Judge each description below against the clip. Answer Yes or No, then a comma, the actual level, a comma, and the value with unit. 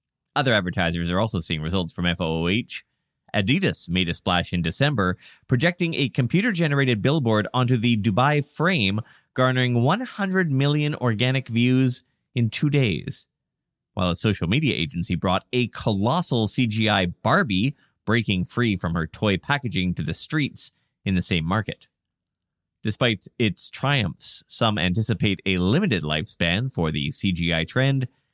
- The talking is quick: No, average, 140 wpm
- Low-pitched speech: Yes, low, 110 Hz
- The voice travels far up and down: Yes, wide, 6.2 semitones